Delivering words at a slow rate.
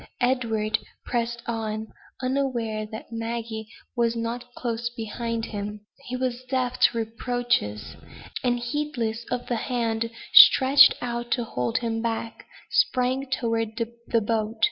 Yes: slow, 125 wpm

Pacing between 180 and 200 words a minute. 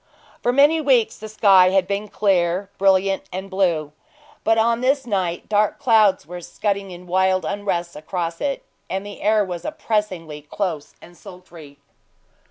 No: average, 155 wpm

